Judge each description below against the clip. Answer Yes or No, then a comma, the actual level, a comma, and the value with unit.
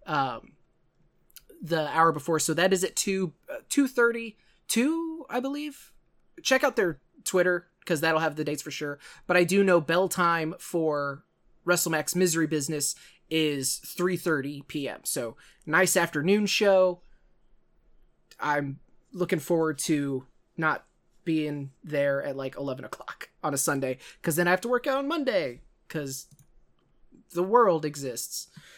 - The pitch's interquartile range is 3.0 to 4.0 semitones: No, average, 4.4 semitones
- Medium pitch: Yes, medium, 170 Hz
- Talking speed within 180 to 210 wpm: No, average, 150 wpm